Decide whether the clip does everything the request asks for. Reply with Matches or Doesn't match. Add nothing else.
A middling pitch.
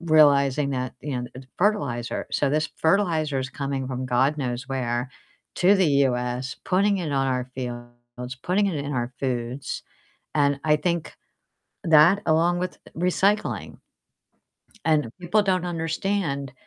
Matches